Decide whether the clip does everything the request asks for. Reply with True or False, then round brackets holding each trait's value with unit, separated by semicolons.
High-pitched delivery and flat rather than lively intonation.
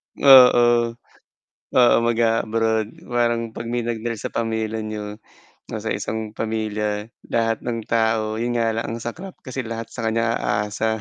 False (115 Hz; 1.2 semitones)